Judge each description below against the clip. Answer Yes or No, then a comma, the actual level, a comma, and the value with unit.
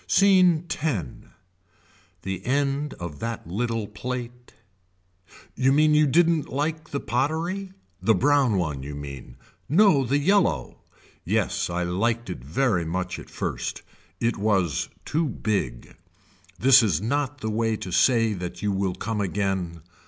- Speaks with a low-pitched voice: Yes, low, 115 Hz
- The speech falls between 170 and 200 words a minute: No, average, 140 wpm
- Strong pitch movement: Yes, wide, 7.7 semitones